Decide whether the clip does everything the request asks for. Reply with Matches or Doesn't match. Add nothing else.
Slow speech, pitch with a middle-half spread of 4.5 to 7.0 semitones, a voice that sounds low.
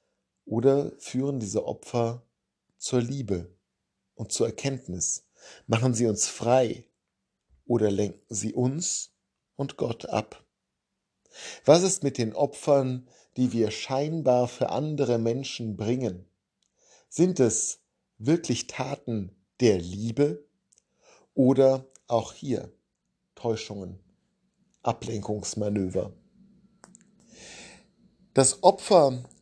Matches